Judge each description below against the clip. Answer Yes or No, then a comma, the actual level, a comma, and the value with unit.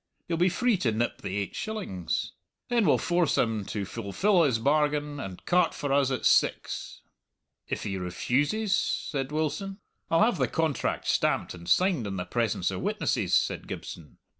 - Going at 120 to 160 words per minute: No, average, 170 wpm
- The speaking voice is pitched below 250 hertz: Yes, medium, 140 Hz